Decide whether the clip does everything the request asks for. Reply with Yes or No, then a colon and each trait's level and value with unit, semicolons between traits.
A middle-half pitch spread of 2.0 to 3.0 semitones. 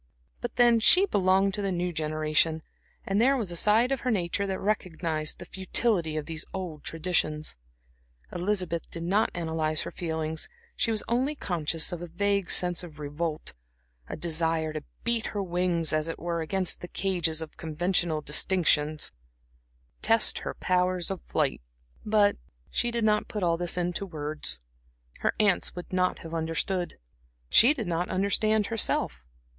No: average, 3.8 semitones